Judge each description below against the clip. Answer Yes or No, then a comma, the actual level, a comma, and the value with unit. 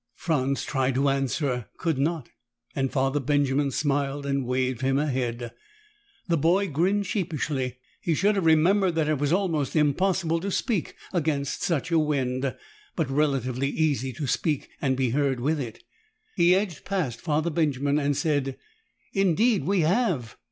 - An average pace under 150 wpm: No, average, 155 wpm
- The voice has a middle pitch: Yes, medium, 145 Hz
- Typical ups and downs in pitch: Yes, average, 3.9 semitones